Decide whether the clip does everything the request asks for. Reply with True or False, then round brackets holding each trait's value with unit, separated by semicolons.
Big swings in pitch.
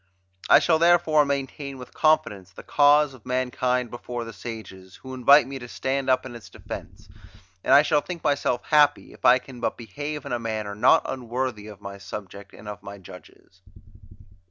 False (4.7 semitones)